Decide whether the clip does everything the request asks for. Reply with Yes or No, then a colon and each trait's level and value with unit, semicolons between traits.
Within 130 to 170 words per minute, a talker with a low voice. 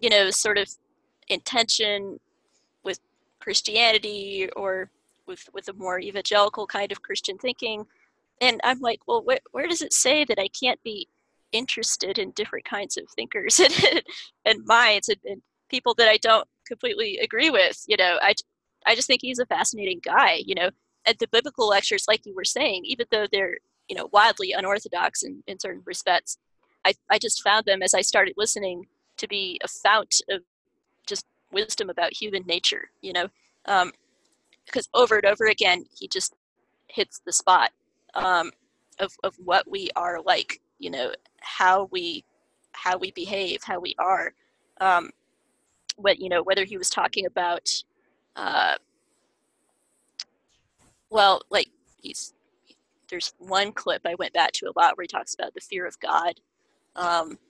No: average, 165 wpm; high, 220 Hz